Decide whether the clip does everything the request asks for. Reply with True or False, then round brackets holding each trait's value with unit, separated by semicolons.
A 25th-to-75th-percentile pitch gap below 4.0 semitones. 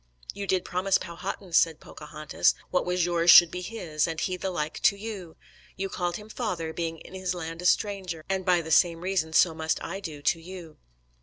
True (2.5 semitones)